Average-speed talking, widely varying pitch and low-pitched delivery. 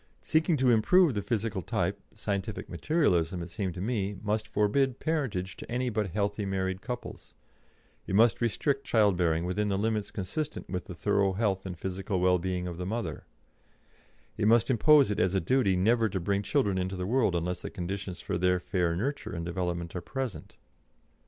No: average, 185 wpm; average, 4.0 semitones; low, 100 Hz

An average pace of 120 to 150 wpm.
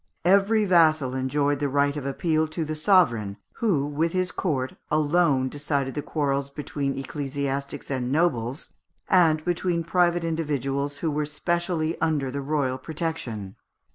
Yes: average, 140 wpm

